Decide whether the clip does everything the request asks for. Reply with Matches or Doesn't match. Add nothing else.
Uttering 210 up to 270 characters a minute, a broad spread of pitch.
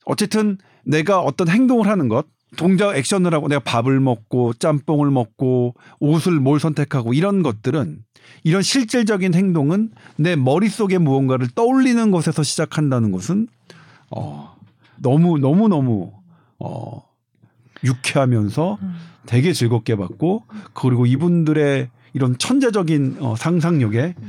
Doesn't match